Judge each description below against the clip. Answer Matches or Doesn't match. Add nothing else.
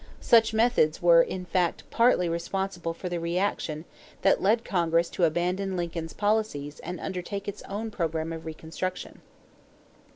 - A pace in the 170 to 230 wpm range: Doesn't match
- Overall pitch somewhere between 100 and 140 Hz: Doesn't match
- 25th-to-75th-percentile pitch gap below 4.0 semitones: Matches